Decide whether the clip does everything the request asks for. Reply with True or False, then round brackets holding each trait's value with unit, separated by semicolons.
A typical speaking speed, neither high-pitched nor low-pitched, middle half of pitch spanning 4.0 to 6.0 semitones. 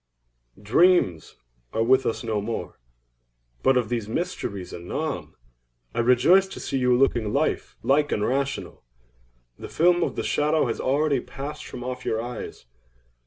False (150 wpm; 130 Hz; 4.5 semitones)